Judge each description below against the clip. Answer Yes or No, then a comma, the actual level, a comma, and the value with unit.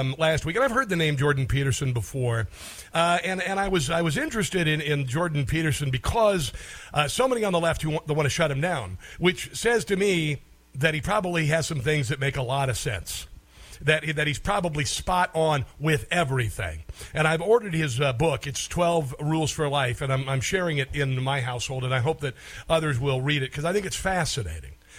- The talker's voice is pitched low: No, medium, 150 Hz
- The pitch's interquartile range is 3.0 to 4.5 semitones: Yes, average, 4.1 semitones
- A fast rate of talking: Yes, fast, 225 wpm